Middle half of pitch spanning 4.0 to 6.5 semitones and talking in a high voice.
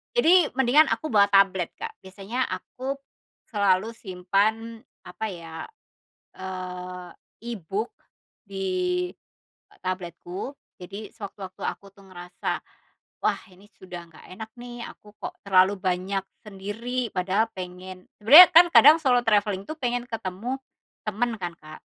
Yes: average, 4.3 semitones; high, 200 Hz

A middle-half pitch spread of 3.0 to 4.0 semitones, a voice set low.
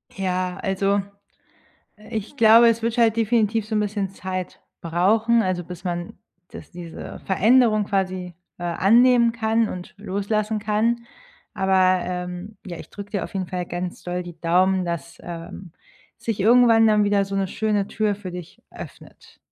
No: average, 3.3 semitones; high, 195 Hz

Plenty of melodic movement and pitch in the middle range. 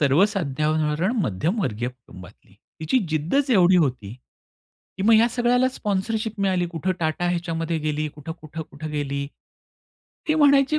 Yes: wide, 5.9 semitones; medium, 165 Hz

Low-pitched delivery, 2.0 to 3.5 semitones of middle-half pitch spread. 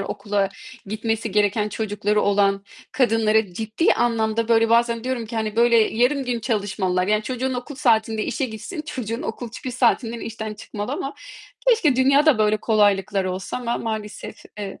No: high, 225 Hz; narrow, 2.6 semitones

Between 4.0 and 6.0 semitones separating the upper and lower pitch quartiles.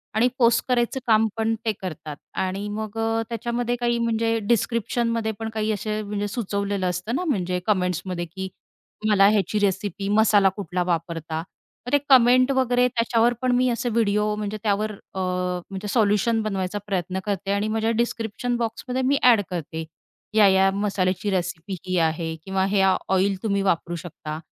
No: average, 3.3 semitones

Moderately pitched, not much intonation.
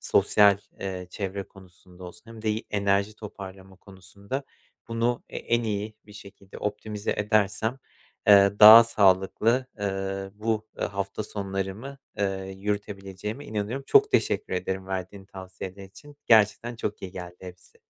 No: low, 100 Hz; narrow, 2.1 semitones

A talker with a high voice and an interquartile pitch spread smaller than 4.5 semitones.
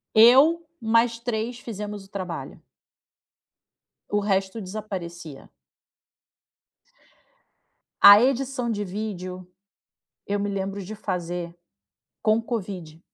Yes: high, 205 Hz; average, 3.7 semitones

